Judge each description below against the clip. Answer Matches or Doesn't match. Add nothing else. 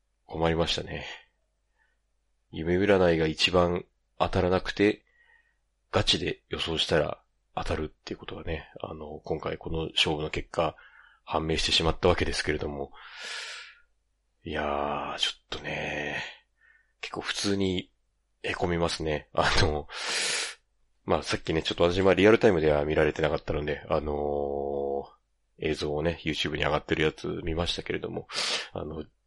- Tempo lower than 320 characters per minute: Matches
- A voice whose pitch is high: Doesn't match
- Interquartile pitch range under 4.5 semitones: Matches